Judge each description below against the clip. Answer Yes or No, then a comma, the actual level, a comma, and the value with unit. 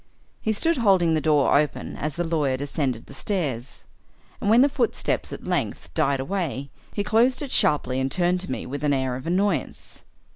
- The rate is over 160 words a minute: Yes, average, 190 wpm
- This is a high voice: No, medium, 155 Hz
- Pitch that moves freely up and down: Yes, wide, 6.5 semitones